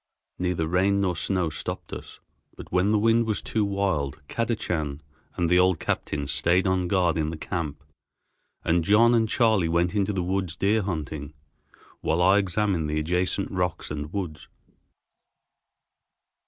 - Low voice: Yes, very low, 90 Hz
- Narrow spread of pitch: No, average, 3.8 semitones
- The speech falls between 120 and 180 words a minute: Yes, average, 155 wpm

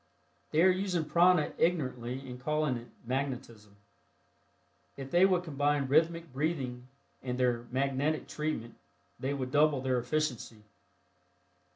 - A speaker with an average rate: No, slow, 125 wpm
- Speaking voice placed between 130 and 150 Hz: Yes, medium, 140 Hz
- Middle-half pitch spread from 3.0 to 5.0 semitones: Yes, average, 3.8 semitones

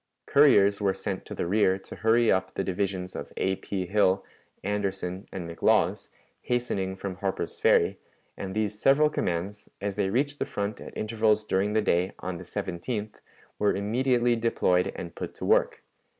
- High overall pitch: No, low, 100 Hz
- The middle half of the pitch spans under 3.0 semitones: Yes, narrow, 2.5 semitones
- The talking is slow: No, average, 170 wpm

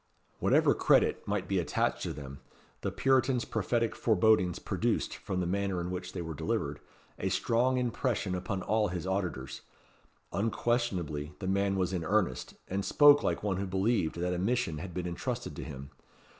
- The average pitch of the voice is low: Yes, very low, 95 Hz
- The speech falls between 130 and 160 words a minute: No, average, 170 wpm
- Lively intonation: No, average, 4.1 semitones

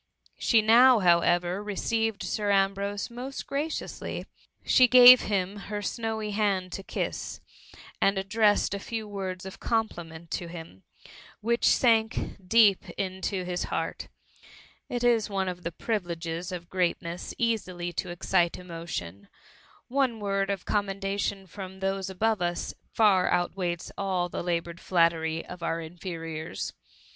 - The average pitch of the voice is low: No, high, 195 Hz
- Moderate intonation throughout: Yes, average, 3.5 semitones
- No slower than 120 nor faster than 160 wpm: Yes, slow, 135 wpm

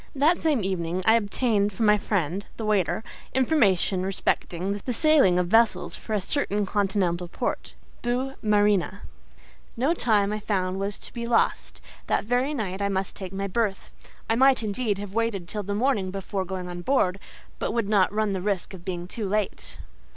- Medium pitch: No, high, 205 Hz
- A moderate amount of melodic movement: Yes, average, 3.3 semitones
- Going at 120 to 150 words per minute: No, average, 180 wpm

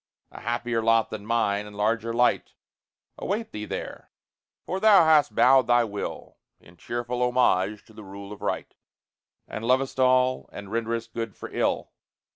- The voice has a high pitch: No, low, 115 Hz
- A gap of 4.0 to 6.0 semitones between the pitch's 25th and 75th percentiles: No, average, 3.2 semitones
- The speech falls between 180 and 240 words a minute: No, average, 160 wpm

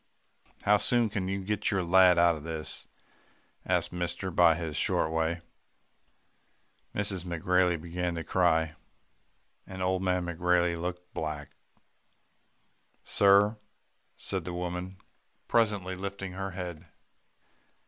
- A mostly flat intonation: Yes, narrow, 1.8 semitones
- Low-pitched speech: Yes, very low, 90 Hz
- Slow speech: Yes, slow, 120 wpm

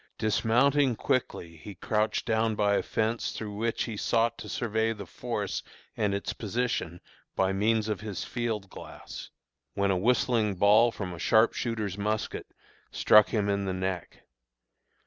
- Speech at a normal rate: Yes, average, 150 wpm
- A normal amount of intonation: No, narrow, 2.3 semitones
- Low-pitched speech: Yes, low, 105 Hz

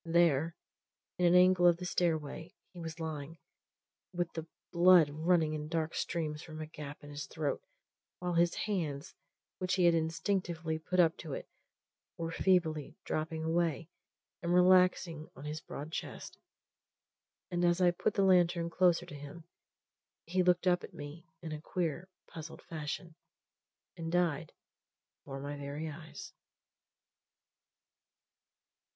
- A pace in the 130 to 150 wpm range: Yes, average, 145 wpm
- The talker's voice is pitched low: No, medium, 165 Hz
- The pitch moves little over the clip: Yes, narrow, 2.3 semitones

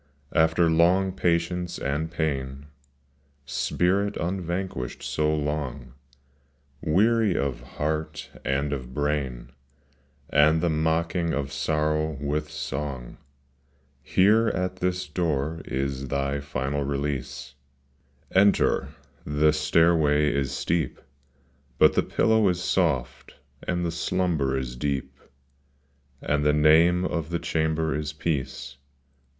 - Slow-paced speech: Yes, slow, 110 wpm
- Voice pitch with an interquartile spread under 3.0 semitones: No, average, 3.4 semitones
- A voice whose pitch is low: Yes, very low, 75 Hz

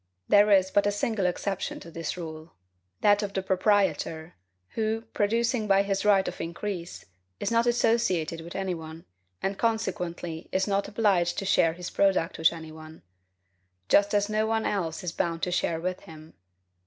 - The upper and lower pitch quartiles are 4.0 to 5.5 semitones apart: No, average, 3.5 semitones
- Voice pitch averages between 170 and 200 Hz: Yes, high, 190 Hz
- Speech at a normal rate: Yes, average, 175 wpm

